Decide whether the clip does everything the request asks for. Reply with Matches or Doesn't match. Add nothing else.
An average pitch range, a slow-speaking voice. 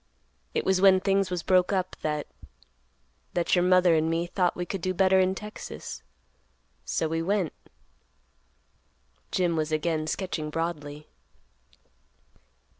Matches